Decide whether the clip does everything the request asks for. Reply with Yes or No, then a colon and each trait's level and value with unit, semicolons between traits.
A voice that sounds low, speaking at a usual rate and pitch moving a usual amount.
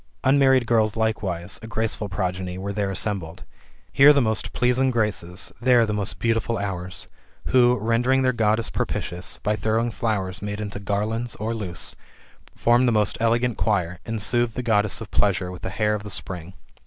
Yes: low, 110 Hz; average, 175 wpm; average, 3.2 semitones